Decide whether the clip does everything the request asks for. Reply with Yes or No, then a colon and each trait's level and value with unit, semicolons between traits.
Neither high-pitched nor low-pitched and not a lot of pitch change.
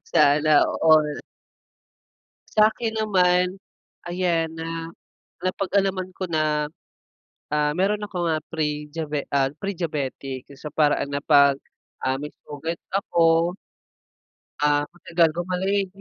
No: medium, 165 Hz; average, 3.5 semitones